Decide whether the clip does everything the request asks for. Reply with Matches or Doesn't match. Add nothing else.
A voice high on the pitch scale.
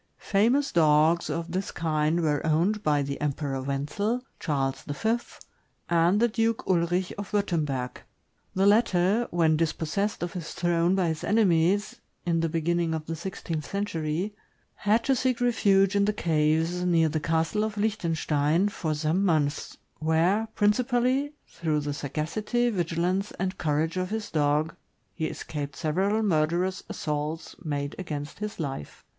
Doesn't match